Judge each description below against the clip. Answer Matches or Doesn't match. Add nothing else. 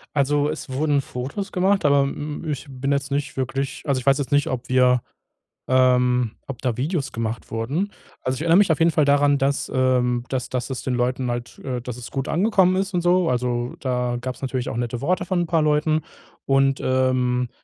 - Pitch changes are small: Doesn't match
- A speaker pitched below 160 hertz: Matches